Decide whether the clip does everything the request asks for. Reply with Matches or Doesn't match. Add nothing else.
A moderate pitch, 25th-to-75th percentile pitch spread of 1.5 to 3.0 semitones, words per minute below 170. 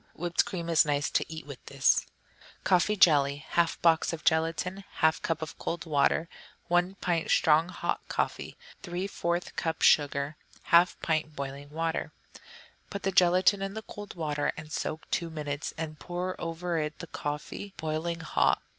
Matches